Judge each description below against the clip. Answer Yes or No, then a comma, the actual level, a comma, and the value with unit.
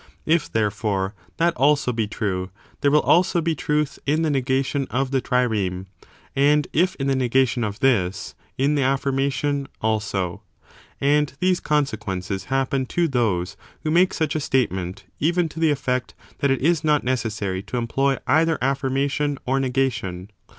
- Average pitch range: Yes, average, 5.0 semitones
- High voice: No, low, 135 Hz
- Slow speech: No, average, 155 wpm